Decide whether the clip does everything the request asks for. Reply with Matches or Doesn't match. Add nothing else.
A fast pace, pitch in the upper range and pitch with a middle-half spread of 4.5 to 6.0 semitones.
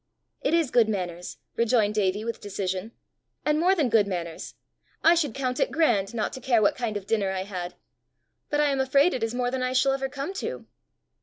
Matches